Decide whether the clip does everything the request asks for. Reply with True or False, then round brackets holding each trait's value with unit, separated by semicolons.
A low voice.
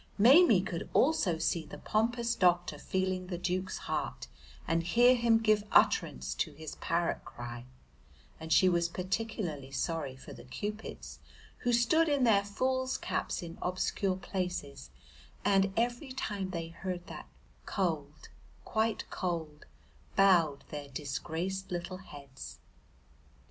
False (185 Hz)